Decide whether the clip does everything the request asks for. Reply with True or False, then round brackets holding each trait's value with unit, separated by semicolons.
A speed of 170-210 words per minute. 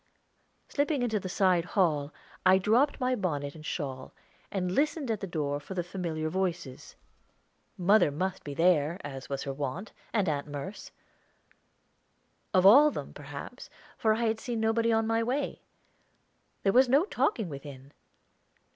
False (155 wpm)